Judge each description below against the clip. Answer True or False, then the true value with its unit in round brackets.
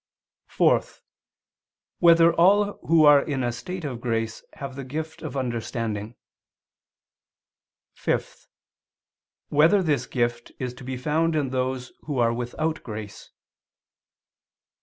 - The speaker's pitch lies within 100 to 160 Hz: True (135 Hz)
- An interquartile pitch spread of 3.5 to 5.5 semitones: True (4.8 semitones)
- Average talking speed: False (115 wpm)